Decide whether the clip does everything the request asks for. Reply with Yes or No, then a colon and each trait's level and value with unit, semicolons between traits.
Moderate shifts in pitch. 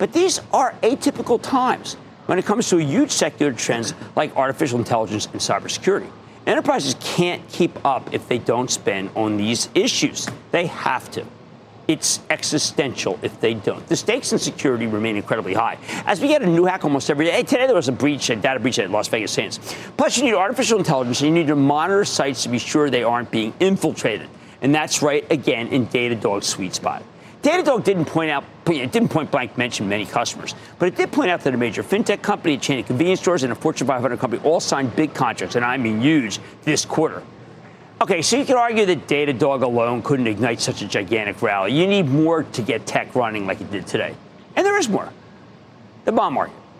No: wide, 7.7 semitones